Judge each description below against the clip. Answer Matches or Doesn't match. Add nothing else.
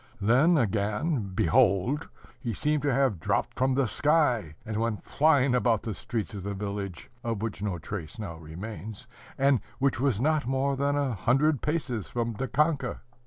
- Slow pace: Doesn't match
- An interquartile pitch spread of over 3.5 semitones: Matches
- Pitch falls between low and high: Doesn't match